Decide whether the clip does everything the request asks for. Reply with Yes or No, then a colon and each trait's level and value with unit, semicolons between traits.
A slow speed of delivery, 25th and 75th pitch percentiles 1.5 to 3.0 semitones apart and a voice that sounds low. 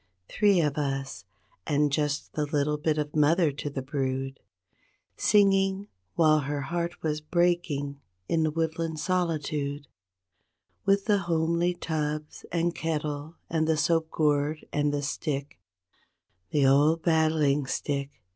No: slow, 130 wpm; narrow, 2.4 semitones; medium, 150 Hz